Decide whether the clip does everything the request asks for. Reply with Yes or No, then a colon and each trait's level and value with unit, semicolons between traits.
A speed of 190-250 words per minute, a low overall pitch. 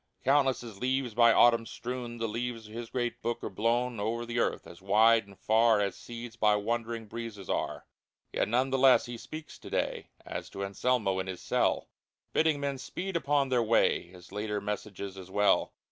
Yes: average, 195 wpm; low, 115 Hz